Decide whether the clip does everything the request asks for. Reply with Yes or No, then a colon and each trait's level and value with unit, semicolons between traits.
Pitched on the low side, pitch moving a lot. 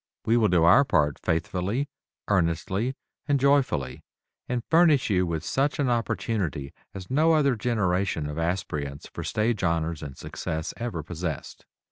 Yes: very low, 95 Hz; wide, 7.2 semitones